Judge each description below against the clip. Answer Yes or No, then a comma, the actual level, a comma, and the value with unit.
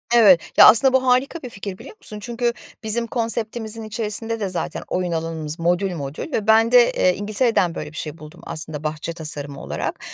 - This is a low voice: No, high, 205 Hz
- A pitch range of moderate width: No, wide, 5.9 semitones